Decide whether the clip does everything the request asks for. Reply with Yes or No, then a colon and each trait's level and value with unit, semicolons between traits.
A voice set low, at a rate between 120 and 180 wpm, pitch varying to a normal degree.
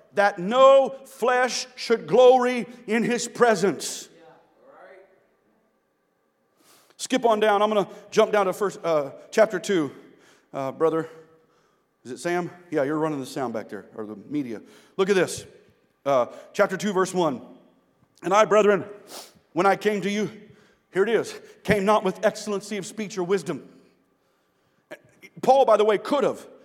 No: high, 205 Hz; average, 155 wpm; average, 4.4 semitones